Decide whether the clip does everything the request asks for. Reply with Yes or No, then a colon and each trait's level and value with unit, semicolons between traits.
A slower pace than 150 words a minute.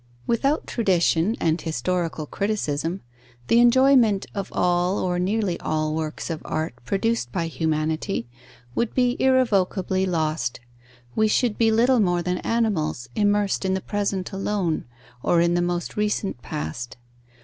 Yes: average, 140 wpm